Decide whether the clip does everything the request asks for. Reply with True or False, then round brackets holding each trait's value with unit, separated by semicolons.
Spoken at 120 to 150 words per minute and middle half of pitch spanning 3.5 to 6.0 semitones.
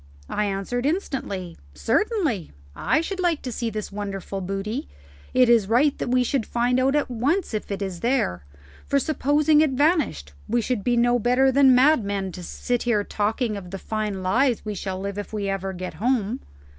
False (190 wpm; 5.2 semitones)